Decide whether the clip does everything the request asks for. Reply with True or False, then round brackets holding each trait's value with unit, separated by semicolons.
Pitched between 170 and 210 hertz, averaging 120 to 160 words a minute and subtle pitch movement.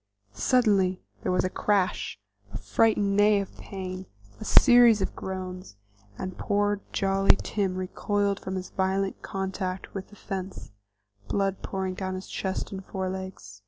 True (190 Hz; 145 wpm; 1.3 semitones)